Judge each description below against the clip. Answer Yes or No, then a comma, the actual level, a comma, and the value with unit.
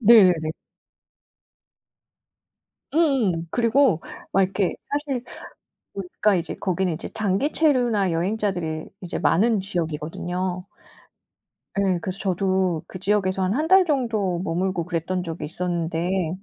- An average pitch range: Yes, average, 3.5 semitones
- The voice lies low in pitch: No, medium, 185 Hz